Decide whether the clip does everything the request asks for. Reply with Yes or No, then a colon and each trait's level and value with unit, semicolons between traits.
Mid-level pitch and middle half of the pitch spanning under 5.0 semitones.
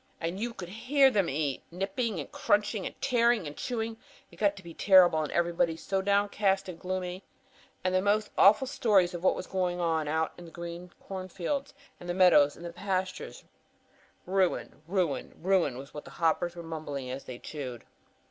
Yes: medium, 180 Hz; average, 3.3 semitones